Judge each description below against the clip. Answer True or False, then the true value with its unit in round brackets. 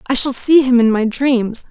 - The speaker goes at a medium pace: False (245 wpm)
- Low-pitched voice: False (250 Hz)